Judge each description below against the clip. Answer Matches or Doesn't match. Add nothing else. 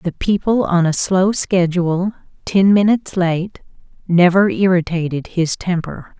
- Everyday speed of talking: Doesn't match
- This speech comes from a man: Doesn't match